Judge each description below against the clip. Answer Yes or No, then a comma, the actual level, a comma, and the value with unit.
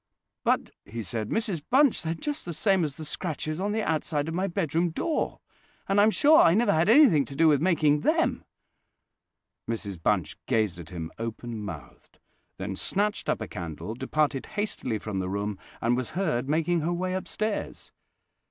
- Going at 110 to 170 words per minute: No, average, 180 wpm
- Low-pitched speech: No, medium, 155 Hz